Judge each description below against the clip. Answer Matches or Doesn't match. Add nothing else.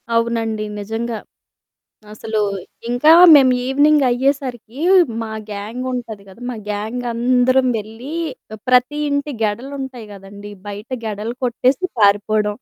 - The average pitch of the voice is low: Doesn't match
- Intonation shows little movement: Doesn't match